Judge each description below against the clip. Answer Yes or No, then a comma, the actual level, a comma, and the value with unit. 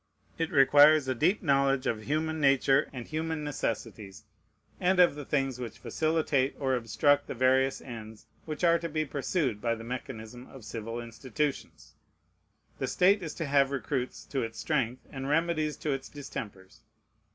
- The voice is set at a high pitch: No, low, 135 Hz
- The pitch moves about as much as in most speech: Yes, average, 4.3 semitones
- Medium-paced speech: Yes, average, 165 wpm